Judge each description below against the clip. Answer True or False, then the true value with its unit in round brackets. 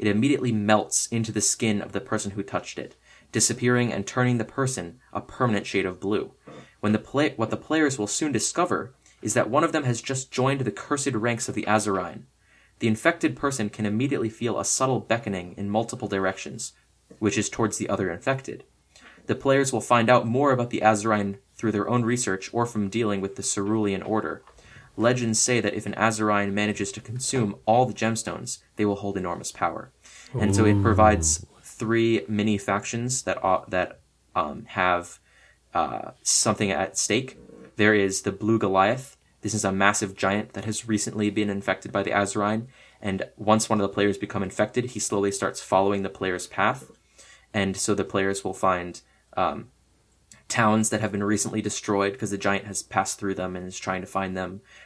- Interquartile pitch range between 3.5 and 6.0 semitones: False (2.6 semitones)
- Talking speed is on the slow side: False (190 wpm)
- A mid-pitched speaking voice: False (105 Hz)